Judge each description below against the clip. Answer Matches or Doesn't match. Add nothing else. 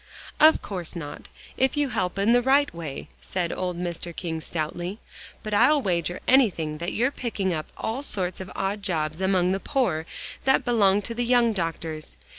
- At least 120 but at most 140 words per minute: Doesn't match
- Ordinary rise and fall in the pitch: Doesn't match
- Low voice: Doesn't match